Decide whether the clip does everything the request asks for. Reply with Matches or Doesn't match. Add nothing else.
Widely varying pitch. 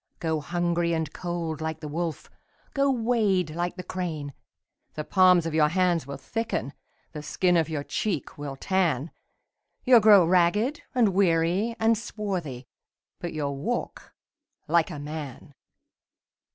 Doesn't match